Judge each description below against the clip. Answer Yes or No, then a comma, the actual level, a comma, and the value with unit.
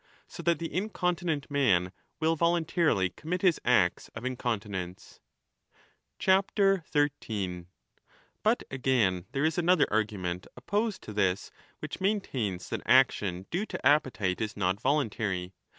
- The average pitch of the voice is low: Yes, low, 130 Hz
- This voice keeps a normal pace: No, slow, 130 wpm